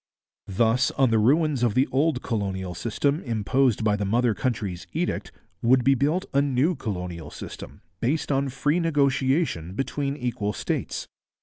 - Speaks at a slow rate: No, average, 150 wpm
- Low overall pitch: Yes, low, 125 Hz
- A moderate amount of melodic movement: Yes, average, 4.9 semitones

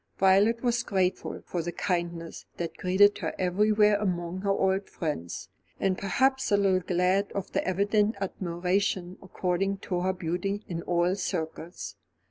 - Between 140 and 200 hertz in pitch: Yes, high, 190 Hz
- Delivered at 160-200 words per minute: No, average, 145 wpm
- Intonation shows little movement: Yes, narrow, 2.3 semitones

